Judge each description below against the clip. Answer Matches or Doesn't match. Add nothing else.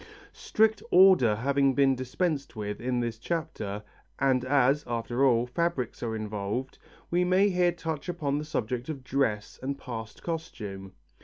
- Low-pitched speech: Matches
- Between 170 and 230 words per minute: Doesn't match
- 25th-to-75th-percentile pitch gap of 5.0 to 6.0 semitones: Matches